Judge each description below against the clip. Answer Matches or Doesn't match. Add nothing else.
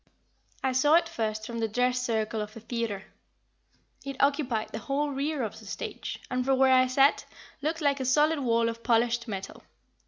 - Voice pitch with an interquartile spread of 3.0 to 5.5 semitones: Matches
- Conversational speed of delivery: Matches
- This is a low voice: Doesn't match